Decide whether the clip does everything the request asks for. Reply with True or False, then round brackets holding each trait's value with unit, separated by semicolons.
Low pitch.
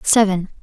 False (195 Hz)